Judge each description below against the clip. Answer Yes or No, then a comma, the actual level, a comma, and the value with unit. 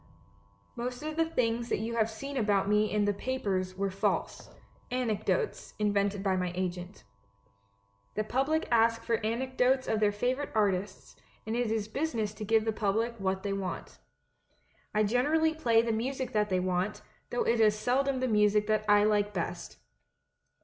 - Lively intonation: No, average, 3.3 semitones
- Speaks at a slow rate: No, average, 170 wpm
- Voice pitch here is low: No, high, 220 Hz